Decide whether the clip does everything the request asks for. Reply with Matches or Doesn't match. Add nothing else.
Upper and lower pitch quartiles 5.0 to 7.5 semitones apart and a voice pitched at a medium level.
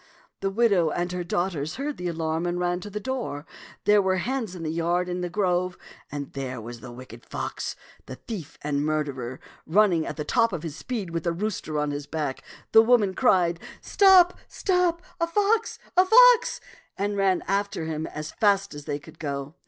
Matches